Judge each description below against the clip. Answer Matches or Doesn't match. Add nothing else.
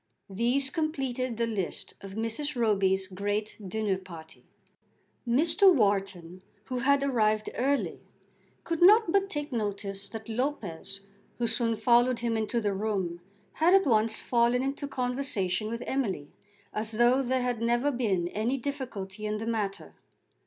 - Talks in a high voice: Matches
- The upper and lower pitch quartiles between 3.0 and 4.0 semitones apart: Doesn't match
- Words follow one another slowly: Doesn't match